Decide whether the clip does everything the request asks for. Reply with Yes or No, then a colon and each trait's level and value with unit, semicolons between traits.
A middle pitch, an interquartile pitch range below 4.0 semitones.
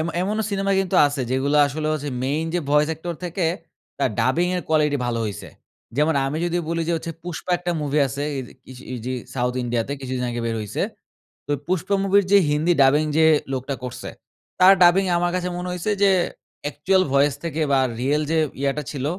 No: medium, 150 Hz; average, 4.7 semitones